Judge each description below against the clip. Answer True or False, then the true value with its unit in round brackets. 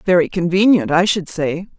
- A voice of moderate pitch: True (175 Hz)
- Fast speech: False (170 wpm)